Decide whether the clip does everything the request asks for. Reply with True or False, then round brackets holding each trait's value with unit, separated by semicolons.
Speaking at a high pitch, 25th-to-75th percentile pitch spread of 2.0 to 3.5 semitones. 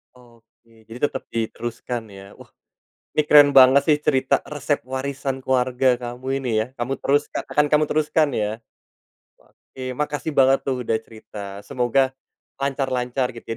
False (130 Hz; 2.6 semitones)